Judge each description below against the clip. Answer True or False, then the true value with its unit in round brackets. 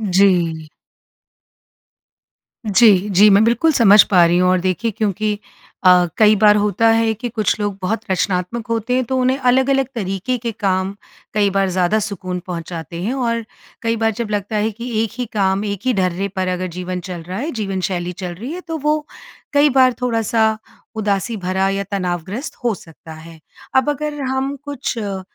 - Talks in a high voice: True (210 Hz)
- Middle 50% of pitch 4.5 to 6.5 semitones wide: False (4.1 semitones)